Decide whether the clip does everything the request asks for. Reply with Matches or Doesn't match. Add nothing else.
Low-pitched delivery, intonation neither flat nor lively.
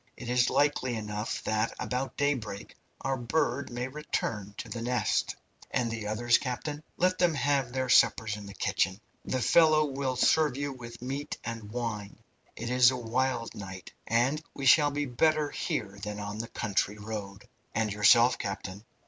Matches